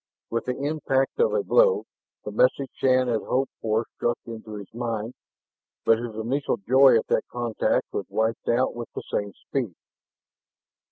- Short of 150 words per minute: No, average, 165 wpm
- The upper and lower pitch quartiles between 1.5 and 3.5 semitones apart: Yes, average, 3.1 semitones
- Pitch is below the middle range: Yes, low, 120 Hz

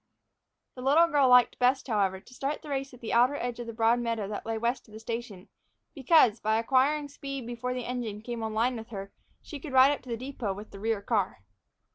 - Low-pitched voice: No, high, 240 Hz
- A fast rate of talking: Yes, fast, 240 wpm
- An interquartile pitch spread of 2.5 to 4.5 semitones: Yes, average, 3.2 semitones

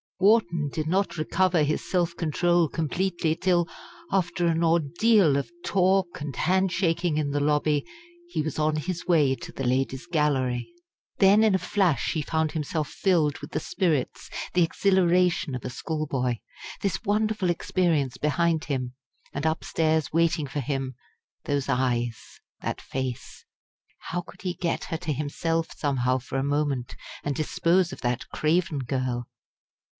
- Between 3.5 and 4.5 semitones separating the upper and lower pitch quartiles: Yes, average, 4.0 semitones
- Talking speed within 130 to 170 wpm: Yes, average, 150 wpm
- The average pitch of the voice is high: No, medium, 160 Hz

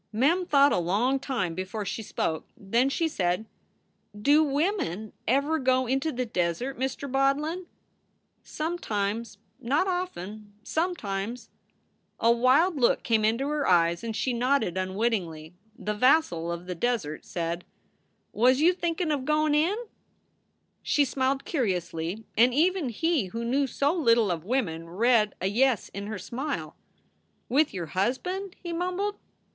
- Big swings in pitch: Yes, wide, 6.9 semitones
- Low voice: No, high, 245 Hz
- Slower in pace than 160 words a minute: Yes, average, 140 wpm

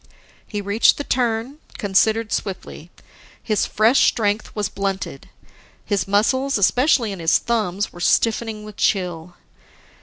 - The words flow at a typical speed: No, slow, 125 wpm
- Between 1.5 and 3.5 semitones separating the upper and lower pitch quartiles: Yes, average, 2.7 semitones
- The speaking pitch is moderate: No, high, 210 Hz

